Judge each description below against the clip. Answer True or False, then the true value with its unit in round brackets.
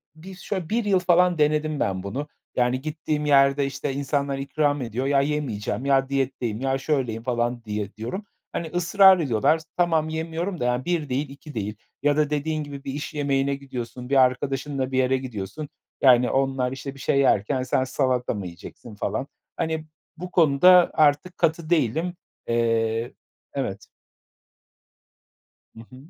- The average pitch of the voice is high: False (140 Hz)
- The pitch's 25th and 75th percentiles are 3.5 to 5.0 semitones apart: True (3.8 semitones)